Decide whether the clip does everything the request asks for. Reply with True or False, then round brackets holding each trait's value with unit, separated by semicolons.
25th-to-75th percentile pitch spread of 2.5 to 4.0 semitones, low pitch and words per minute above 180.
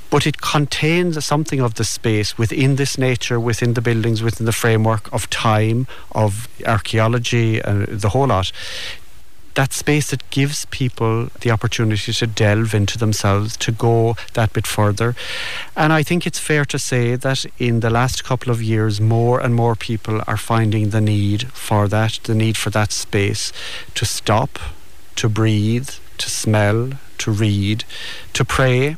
False (2.8 semitones; 115 Hz; 165 wpm)